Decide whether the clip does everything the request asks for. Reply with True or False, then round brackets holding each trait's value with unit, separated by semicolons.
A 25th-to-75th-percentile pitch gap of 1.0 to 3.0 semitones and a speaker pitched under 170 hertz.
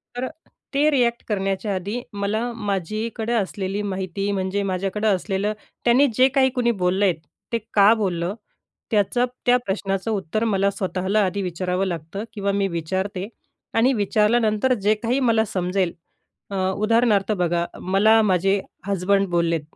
False (2.7 semitones; 200 Hz)